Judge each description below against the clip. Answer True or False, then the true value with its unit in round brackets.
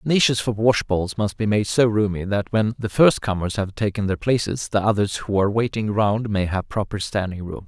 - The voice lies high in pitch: False (105 Hz)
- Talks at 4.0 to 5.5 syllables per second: True (5.2 syllables/s)